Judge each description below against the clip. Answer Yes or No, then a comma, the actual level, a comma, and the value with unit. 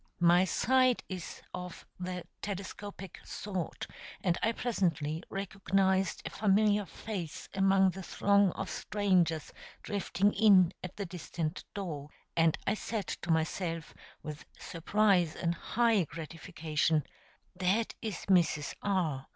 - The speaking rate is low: Yes, slow, 120 wpm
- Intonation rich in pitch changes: No, average, 3.4 semitones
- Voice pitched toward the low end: No, medium, 185 Hz